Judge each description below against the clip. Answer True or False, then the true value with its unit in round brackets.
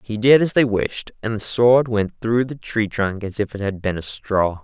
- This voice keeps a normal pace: False (260 wpm)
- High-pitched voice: False (110 Hz)